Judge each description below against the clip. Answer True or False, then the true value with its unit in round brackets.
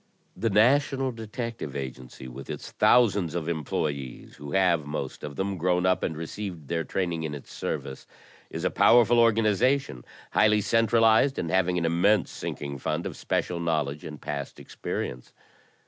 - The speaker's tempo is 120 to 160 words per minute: True (155 wpm)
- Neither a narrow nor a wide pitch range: False (6.6 semitones)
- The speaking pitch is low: True (90 Hz)